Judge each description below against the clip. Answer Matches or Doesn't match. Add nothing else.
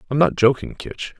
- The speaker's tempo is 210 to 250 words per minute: Doesn't match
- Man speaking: Matches